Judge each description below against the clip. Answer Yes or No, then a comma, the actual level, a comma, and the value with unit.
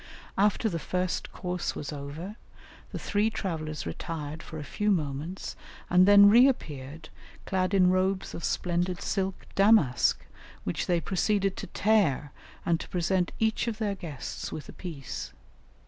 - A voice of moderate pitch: Yes, medium, 180 Hz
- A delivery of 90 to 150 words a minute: Yes, average, 145 wpm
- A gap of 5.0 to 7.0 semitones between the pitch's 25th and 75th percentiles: No, average, 4.3 semitones